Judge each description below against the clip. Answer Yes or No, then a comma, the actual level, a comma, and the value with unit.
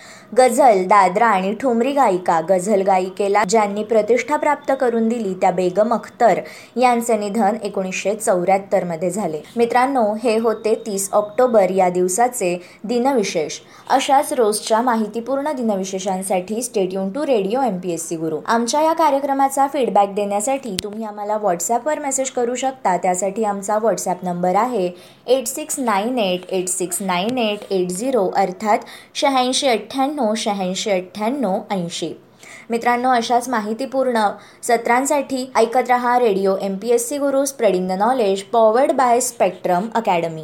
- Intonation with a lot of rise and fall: No, average, 4.3 semitones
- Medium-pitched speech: No, high, 220 Hz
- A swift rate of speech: Yes, fast, 140 wpm